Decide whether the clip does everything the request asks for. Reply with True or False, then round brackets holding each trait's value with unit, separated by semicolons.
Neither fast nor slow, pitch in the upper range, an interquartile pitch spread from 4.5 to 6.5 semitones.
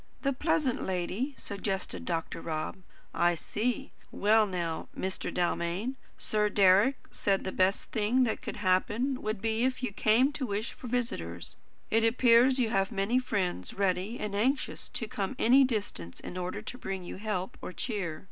True (165 wpm; 210 Hz; 4.8 semitones)